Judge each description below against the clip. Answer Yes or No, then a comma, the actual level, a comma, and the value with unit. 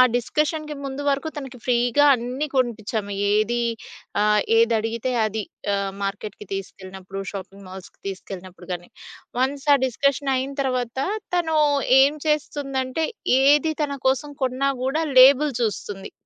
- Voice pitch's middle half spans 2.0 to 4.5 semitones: No, average, 5.0 semitones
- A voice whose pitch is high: Yes, very high, 250 Hz